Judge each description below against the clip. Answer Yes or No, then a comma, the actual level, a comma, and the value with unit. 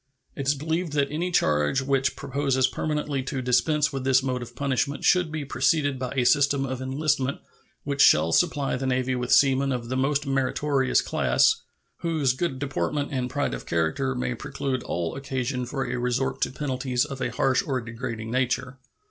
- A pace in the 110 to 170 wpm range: No, average, 180 wpm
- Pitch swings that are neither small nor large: No, narrow, 2.1 semitones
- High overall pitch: No, low, 135 Hz